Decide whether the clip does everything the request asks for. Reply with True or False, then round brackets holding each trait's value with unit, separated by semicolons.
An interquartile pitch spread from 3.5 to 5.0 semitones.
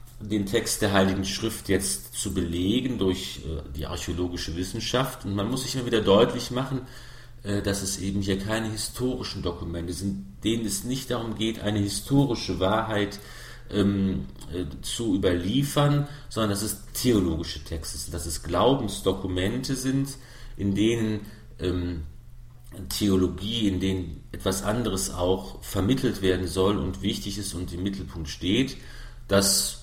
True (3.9 semitones)